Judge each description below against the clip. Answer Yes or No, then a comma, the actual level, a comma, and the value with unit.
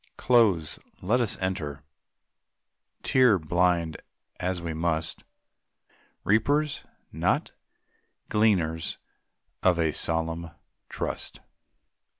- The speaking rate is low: Yes, slow, 80 wpm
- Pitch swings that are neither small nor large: Yes, average, 4.6 semitones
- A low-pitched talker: Yes, very low, 85 Hz